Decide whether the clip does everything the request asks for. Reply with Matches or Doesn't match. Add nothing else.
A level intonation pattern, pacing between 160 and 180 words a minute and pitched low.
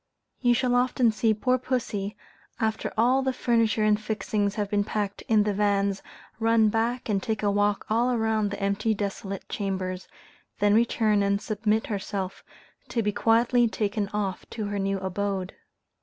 Doesn't match